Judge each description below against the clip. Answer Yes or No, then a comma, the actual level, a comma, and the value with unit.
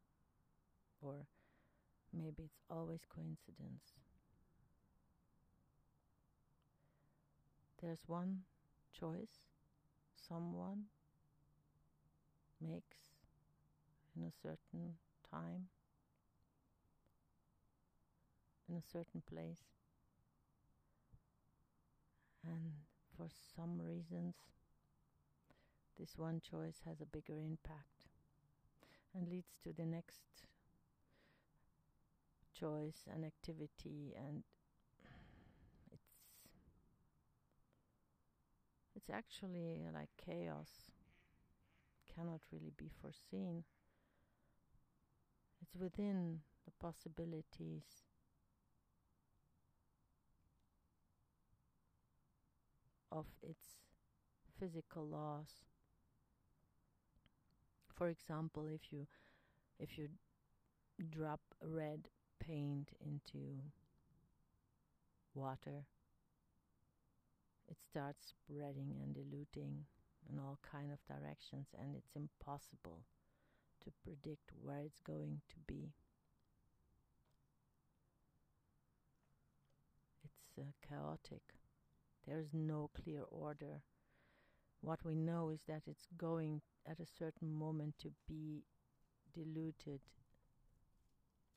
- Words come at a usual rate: No, slow, 70 wpm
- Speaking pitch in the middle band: Yes, medium, 150 Hz